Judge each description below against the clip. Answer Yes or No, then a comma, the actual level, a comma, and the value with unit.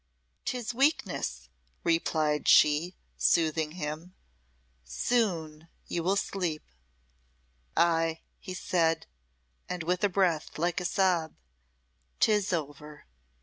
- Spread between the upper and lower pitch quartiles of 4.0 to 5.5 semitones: No, average, 3.1 semitones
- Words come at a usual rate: No, slow, 95 wpm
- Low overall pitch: No, medium, 170 Hz